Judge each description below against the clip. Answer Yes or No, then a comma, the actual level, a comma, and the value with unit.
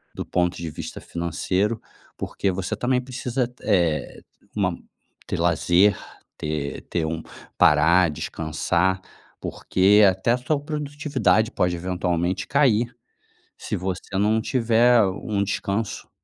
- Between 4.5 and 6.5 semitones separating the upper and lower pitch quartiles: Yes, average, 5.3 semitones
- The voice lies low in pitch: Yes, very low, 95 Hz